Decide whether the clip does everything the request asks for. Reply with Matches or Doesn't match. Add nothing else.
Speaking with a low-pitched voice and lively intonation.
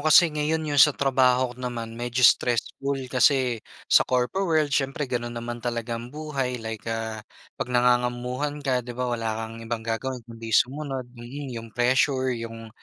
Doesn't match